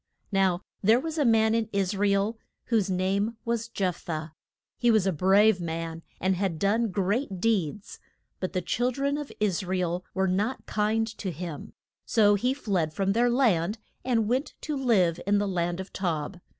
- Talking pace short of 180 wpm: No, average, 190 wpm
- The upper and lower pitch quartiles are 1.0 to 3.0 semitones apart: No, average, 3.8 semitones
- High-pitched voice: Yes, high, 200 Hz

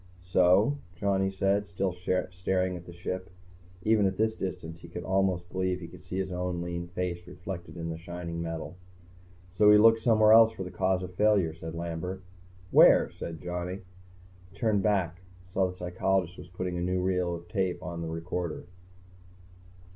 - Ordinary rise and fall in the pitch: No, narrow, 1.8 semitones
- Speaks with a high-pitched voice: No, very low, 90 Hz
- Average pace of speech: Yes, average, 175 wpm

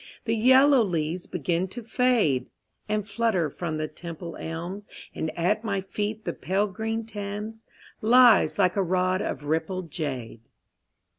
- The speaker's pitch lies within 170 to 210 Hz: Yes, high, 190 Hz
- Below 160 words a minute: Yes, average, 145 wpm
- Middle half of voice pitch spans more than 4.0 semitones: Yes, average, 4.8 semitones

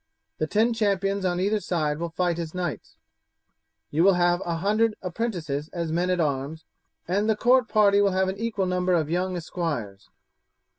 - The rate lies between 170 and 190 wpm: Yes, average, 180 wpm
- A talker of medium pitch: Yes, medium, 180 Hz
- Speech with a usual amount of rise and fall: Yes, average, 3.4 semitones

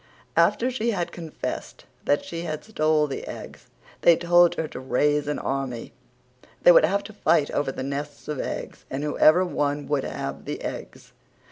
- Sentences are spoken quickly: No, average, 175 wpm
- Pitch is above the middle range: No, medium, 150 Hz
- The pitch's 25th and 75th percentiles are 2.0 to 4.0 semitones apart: Yes, average, 3.3 semitones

